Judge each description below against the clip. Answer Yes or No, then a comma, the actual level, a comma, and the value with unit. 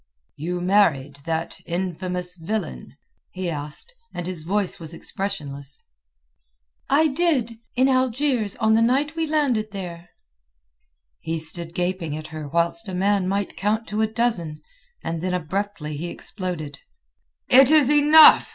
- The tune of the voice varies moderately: No, wide, 5.7 semitones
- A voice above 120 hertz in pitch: Yes, medium, 185 Hz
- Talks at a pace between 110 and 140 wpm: Yes, slow, 135 wpm